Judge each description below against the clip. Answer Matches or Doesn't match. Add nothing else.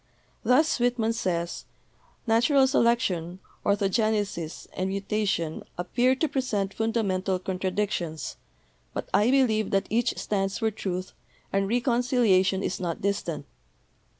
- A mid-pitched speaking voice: Doesn't match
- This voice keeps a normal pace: Doesn't match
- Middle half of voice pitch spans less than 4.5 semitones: Matches